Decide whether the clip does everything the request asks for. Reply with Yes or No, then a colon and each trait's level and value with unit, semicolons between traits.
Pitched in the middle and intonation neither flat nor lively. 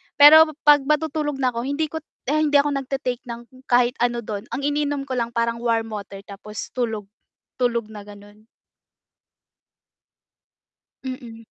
No: high, 245 Hz; average, 4.1 semitones